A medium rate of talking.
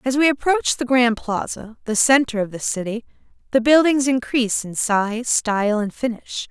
Yes: average, 175 wpm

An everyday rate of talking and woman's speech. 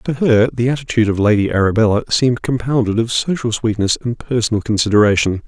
No: average, 165 wpm; male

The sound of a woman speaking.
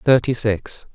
No: male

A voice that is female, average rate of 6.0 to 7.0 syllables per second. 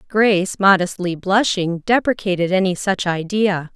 No: female; 4.5 syllables/s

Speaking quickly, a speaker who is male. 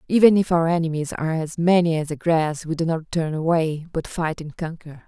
No: fast, 225 wpm; female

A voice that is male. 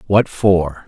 Yes: male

